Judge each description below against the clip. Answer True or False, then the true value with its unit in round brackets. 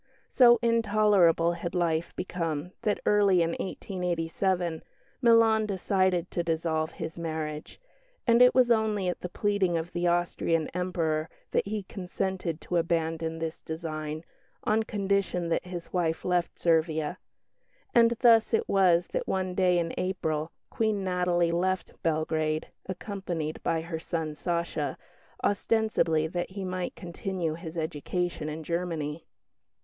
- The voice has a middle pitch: True (175 Hz)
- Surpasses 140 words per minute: False (135 wpm)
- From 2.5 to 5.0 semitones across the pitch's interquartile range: True (2.9 semitones)